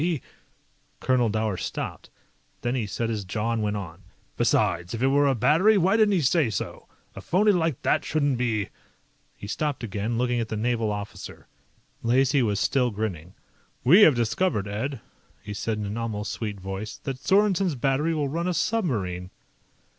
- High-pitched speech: No, low, 120 Hz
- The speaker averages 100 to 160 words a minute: No, average, 185 wpm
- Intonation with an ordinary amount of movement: No, wide, 6.0 semitones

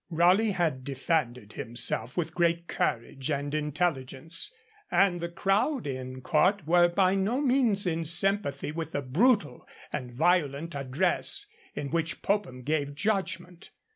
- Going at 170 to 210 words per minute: No, slow, 135 wpm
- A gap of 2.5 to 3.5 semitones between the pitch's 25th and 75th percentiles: No, average, 5.3 semitones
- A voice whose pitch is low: No, medium, 165 Hz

